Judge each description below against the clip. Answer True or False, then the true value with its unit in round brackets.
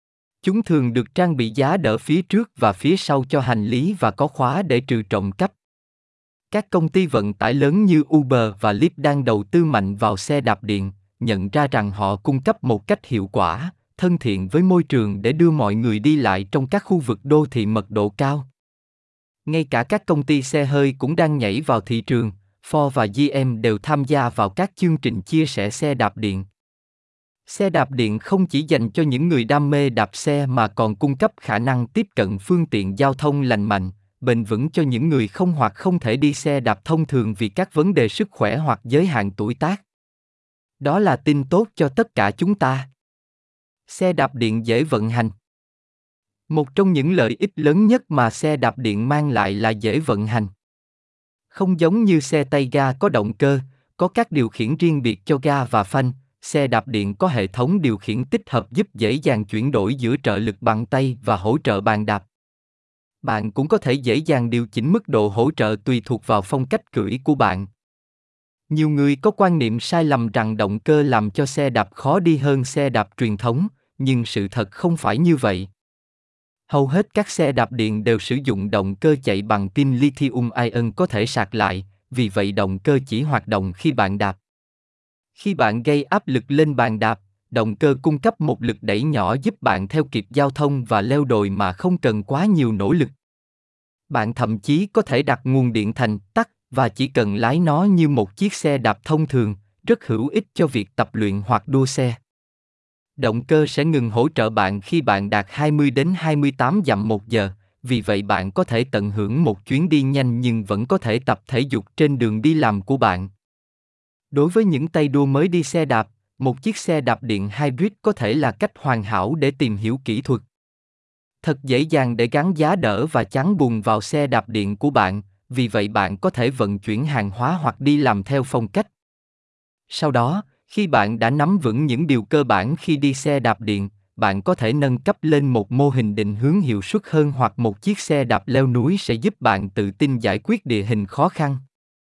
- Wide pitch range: True (5.9 semitones)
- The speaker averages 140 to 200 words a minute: False (215 wpm)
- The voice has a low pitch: True (130 Hz)